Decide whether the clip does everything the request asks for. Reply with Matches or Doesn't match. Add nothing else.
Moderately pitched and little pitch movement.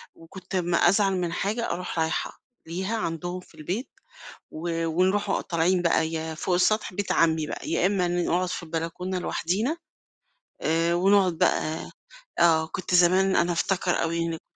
Matches